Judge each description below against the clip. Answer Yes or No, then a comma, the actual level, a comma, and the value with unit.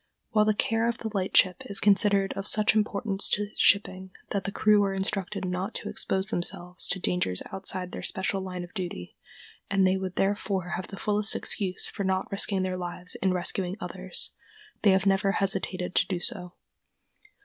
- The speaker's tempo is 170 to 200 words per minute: Yes, average, 180 wpm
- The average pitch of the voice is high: Yes, high, 195 Hz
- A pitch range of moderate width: No, narrow, 1.7 semitones